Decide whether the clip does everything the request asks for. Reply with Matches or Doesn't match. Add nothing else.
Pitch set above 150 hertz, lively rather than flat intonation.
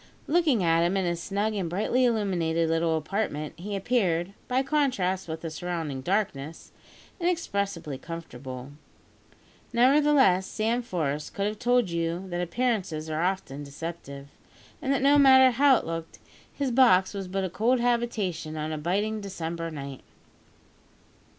Matches